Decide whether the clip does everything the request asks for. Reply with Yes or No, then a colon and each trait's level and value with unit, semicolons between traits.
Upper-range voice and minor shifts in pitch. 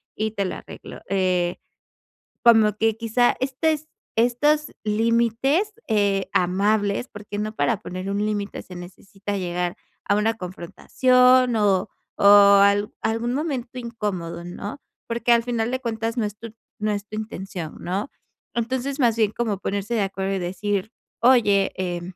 No: high, 215 Hz; average, 3.2 semitones